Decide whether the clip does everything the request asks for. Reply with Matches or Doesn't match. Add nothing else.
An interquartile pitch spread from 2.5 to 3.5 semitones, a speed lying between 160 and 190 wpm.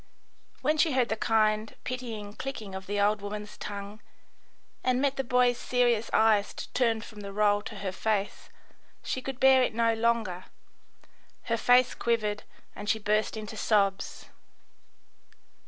Doesn't match